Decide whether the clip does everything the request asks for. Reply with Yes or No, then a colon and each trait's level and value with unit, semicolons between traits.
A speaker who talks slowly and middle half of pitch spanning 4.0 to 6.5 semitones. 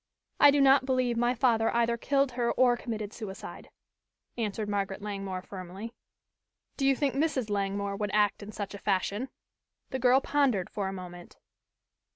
No: average, 165 wpm; average, 4.3 semitones